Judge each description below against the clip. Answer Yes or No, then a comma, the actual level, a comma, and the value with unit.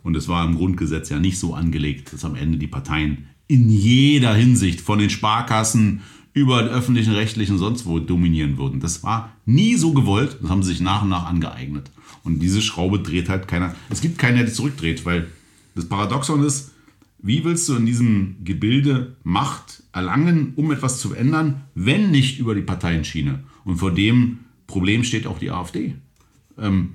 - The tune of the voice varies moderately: No, wide, 6.3 semitones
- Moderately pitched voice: No, low, 105 Hz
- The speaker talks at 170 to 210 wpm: Yes, average, 185 wpm